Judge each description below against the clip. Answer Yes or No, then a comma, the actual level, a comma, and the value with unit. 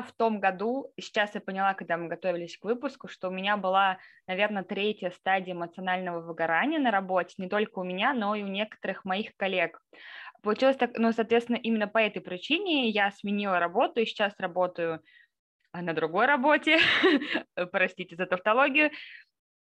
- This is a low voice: No, high, 200 Hz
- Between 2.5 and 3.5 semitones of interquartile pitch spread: No, average, 4.0 semitones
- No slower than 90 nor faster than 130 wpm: No, fast, 160 wpm